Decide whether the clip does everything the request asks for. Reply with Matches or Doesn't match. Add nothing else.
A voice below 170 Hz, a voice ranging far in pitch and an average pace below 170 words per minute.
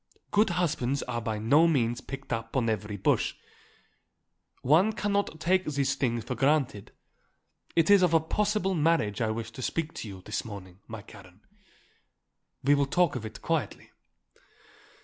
Matches